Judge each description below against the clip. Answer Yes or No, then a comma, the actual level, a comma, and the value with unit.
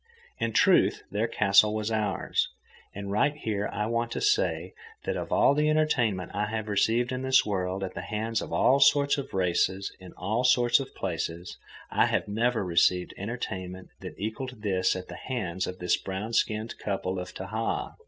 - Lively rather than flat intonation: No, average, 4.2 semitones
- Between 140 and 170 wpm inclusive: No, average, 185 wpm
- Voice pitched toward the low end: Yes, low, 105 Hz